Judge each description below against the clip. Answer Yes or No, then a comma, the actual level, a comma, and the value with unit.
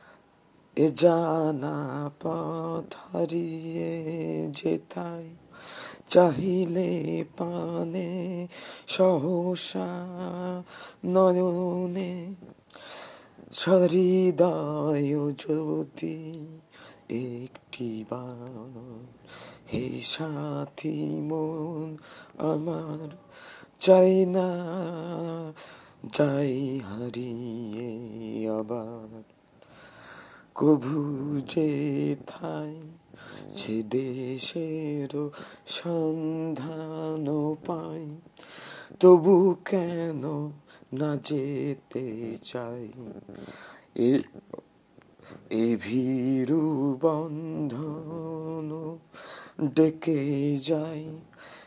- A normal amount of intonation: Yes, average, 4.3 semitones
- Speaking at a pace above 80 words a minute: No, average, 45 wpm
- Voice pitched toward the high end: No, medium, 155 Hz